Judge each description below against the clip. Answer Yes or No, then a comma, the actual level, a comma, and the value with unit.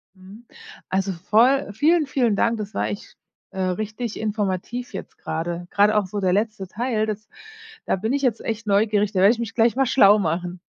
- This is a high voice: Yes, high, 210 Hz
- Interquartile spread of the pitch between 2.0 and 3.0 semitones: No, average, 3.4 semitones